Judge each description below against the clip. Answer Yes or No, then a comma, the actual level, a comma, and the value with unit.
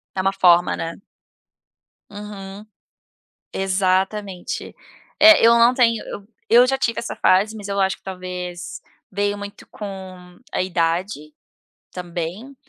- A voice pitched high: Yes, high, 195 Hz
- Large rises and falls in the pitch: No, narrow, 2.6 semitones